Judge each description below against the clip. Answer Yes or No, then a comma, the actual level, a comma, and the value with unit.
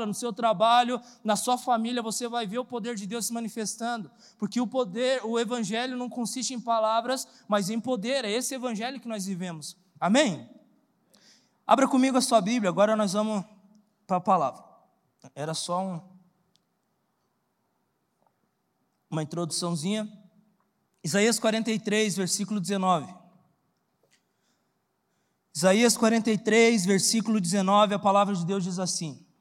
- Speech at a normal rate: Yes, average, 130 wpm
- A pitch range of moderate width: Yes, average, 3.7 semitones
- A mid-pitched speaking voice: No, high, 215 Hz